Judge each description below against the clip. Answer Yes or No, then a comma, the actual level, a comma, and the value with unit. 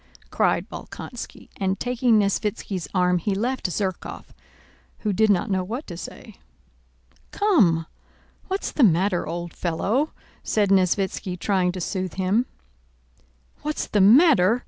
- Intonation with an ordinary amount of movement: Yes, average, 4.2 semitones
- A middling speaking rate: No, slow, 125 wpm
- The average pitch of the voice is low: No, high, 195 Hz